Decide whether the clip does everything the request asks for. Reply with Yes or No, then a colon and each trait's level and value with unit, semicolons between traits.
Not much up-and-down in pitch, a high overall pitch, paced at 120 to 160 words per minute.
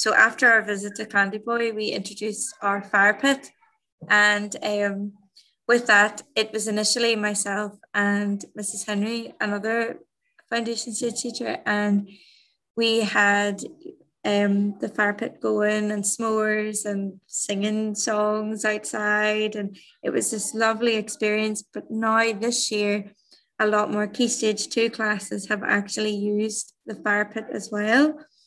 Yes: narrow, 1.6 semitones; high, 215 Hz; average, 140 wpm